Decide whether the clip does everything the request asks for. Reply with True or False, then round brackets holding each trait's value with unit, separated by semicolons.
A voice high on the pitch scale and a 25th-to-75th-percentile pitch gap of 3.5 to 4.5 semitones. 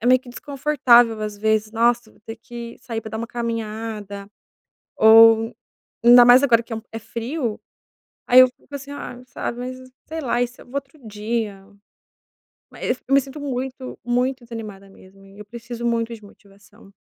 False (235 Hz; 2.4 semitones)